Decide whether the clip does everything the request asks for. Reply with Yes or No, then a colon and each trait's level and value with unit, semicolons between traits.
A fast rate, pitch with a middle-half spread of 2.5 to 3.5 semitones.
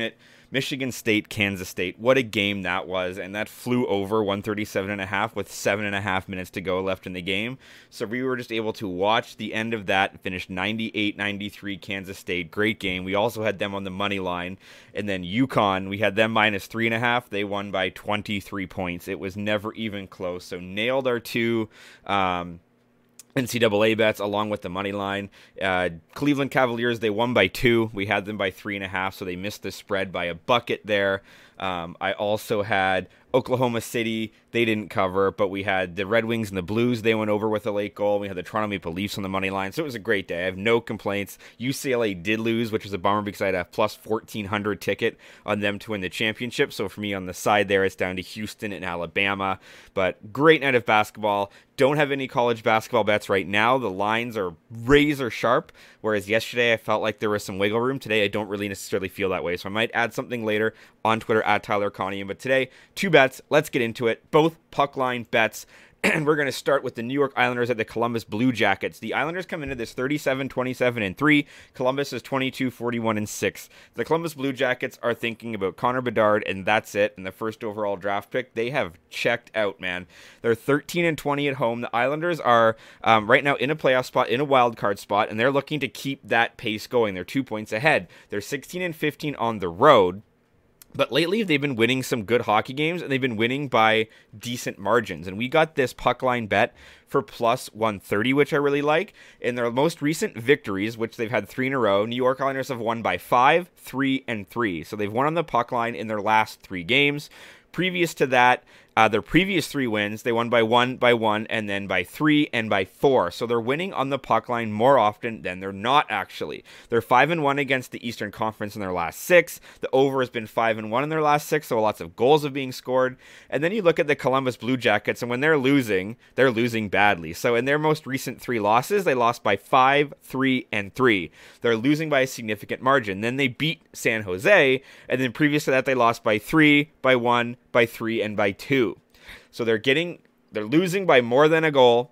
No: fast, 225 wpm; average, 4.2 semitones